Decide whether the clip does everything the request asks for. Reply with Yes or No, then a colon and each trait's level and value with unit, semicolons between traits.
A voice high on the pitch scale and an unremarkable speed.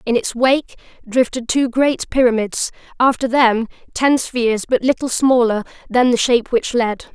Yes: high, 245 Hz; average, 160 wpm